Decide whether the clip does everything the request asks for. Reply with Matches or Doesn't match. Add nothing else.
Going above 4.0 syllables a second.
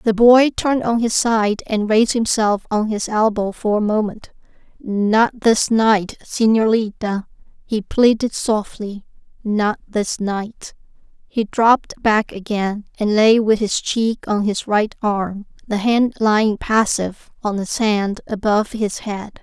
Doesn't match